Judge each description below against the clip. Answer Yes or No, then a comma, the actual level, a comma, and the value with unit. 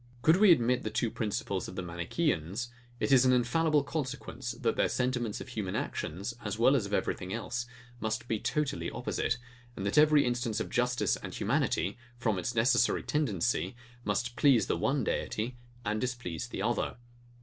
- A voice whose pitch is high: No, low, 120 Hz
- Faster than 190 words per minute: No, average, 175 wpm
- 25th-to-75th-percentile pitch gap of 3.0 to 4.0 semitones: Yes, average, 3.6 semitones